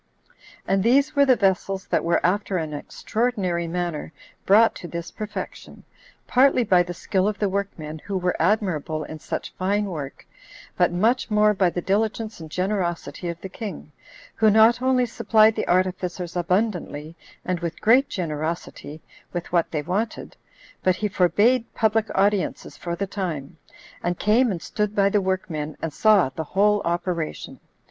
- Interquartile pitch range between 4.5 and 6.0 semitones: No, average, 3.8 semitones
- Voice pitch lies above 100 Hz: Yes, high, 190 Hz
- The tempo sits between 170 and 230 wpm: No, average, 160 wpm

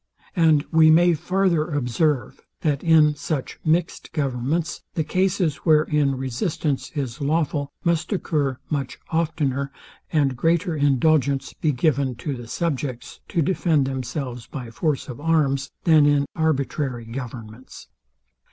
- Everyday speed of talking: No, slow, 125 wpm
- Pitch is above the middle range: No, medium, 145 Hz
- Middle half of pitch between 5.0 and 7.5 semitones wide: No, average, 3.3 semitones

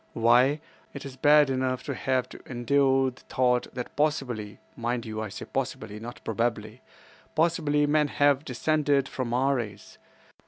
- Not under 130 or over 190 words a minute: Yes, average, 145 wpm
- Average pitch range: Yes, average, 3.2 semitones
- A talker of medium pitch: No, low, 130 Hz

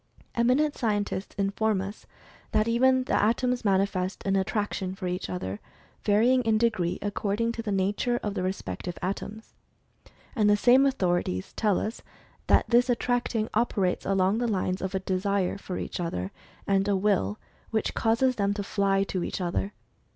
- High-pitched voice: Yes, high, 205 Hz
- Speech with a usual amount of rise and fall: Yes, average, 3.4 semitones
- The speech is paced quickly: No, average, 165 wpm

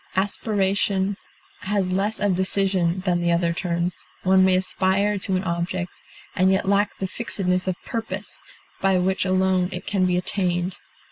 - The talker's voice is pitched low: No, high, 190 Hz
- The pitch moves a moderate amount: No, narrow, 1.4 semitones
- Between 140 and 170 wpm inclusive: Yes, average, 155 wpm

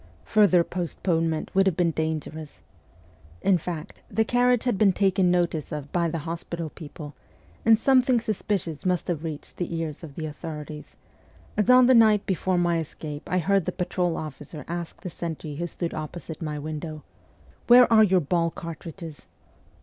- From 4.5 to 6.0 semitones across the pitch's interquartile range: No, average, 3.6 semitones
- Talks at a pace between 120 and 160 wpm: No, average, 170 wpm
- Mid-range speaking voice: Yes, medium, 170 Hz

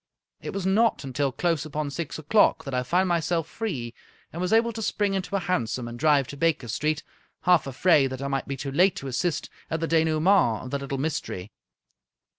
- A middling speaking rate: No, fast, 215 wpm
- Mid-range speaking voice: Yes, medium, 155 Hz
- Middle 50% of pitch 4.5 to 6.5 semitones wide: Yes, average, 4.8 semitones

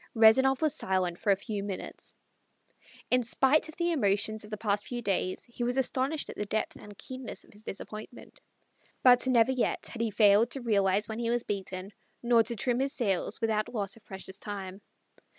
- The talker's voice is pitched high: Yes, high, 220 Hz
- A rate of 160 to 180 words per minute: No, average, 195 wpm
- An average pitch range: Yes, average, 3.6 semitones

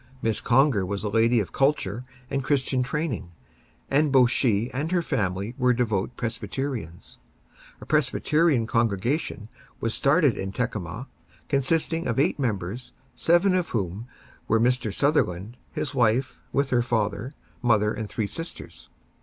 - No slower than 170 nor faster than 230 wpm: No, average, 140 wpm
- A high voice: No, low, 120 Hz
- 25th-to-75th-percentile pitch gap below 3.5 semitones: No, average, 4.5 semitones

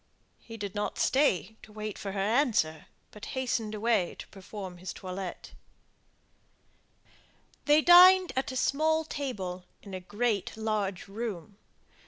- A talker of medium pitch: No, high, 215 Hz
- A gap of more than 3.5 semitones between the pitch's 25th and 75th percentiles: Yes, average, 5.1 semitones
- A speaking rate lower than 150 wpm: Yes, slow, 135 wpm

